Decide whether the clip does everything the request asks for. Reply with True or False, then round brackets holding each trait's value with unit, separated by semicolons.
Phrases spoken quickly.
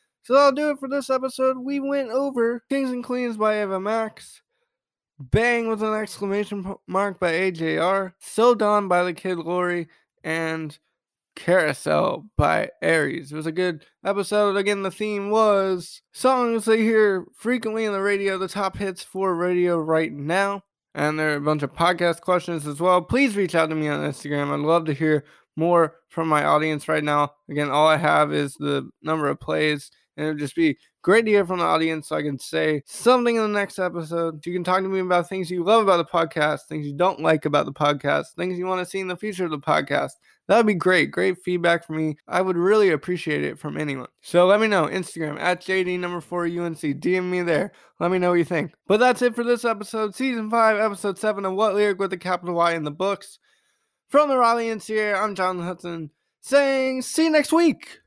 True (215 wpm)